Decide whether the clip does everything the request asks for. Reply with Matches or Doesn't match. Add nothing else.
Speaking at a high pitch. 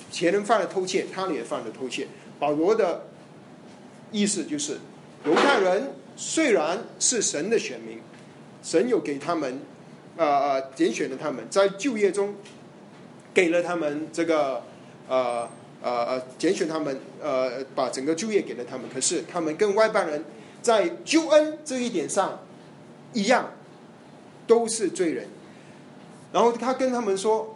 Matches